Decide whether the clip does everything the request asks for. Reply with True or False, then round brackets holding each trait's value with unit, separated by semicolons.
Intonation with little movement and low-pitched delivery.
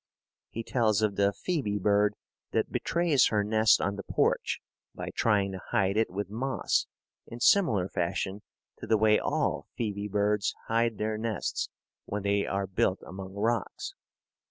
True (2.1 semitones; 105 Hz)